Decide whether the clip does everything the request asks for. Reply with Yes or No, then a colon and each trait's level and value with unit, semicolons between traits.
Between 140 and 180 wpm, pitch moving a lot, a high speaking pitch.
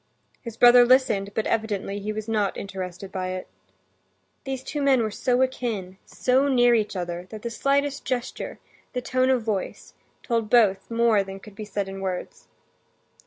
No: average, 170 wpm; average, 4.3 semitones; high, 220 Hz